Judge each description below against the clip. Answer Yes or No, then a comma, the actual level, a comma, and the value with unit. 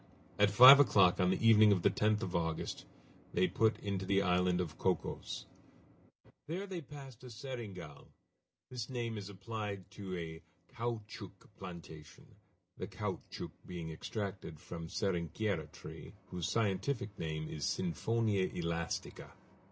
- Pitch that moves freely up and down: No, average, 4.2 semitones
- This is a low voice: Yes, low, 100 Hz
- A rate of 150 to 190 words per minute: No, slow, 135 wpm